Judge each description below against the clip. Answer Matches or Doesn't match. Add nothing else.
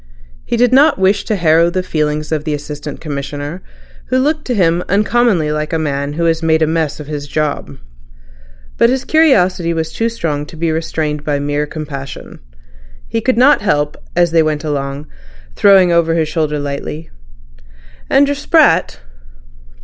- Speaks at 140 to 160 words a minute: Doesn't match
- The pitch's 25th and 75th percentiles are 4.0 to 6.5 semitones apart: Matches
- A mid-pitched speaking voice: Matches